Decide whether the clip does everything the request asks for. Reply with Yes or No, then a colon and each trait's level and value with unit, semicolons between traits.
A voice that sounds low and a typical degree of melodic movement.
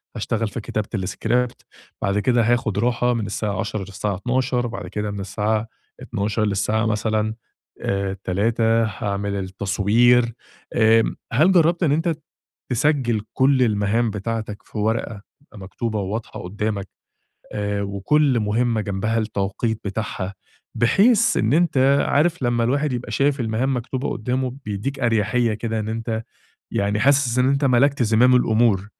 Yes: low, 115 Hz; average, 3.2 semitones